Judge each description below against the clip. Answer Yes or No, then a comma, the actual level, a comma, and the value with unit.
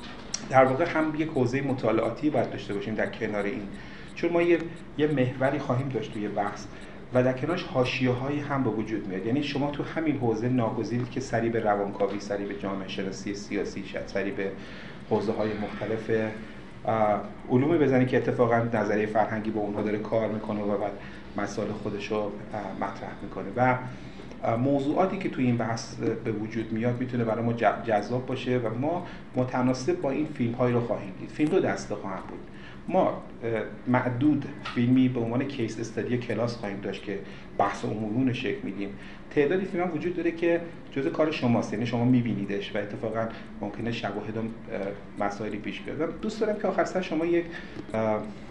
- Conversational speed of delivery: No, fast, 170 wpm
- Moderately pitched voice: No, low, 115 Hz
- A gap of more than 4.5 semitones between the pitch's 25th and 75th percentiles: No, average, 4.0 semitones